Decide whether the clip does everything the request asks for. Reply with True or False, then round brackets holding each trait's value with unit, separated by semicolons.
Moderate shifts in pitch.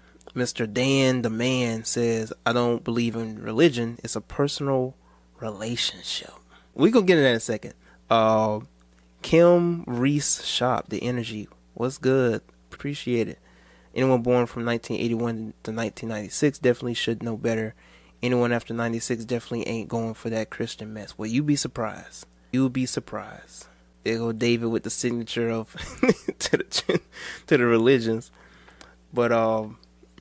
False (2.2 semitones)